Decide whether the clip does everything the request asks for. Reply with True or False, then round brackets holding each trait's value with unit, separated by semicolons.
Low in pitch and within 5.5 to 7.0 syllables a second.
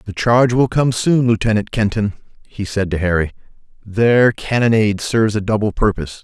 True (105 Hz; 5.6 syllables/s)